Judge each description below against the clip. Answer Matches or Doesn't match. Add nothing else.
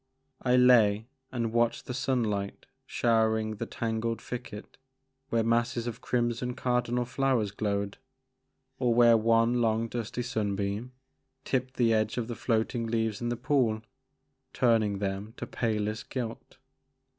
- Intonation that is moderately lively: Doesn't match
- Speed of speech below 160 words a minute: Matches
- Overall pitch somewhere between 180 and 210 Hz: Doesn't match